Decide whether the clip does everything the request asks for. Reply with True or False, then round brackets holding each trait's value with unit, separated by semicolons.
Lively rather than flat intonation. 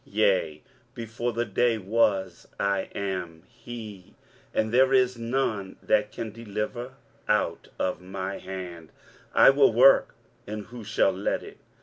False (3.9 semitones)